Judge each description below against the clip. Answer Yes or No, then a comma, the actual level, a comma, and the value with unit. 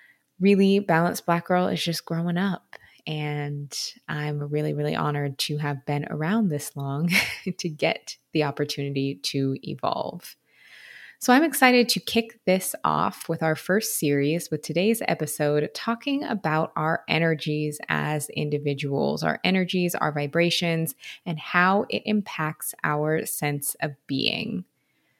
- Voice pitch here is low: No, medium, 160 Hz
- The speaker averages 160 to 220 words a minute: No, slow, 135 wpm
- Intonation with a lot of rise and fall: No, average, 4.1 semitones